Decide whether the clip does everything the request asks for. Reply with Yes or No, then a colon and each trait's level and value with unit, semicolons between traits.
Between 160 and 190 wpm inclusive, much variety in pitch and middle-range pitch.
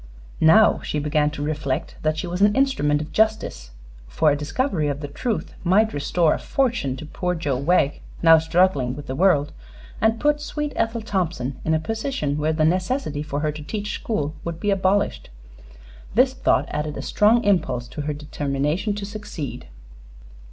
Yes: average, 180 wpm; wide, 6.0 semitones; medium, 160 Hz